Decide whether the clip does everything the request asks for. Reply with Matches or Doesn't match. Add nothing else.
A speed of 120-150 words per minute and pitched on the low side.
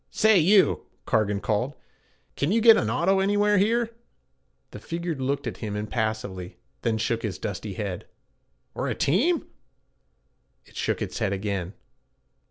Matches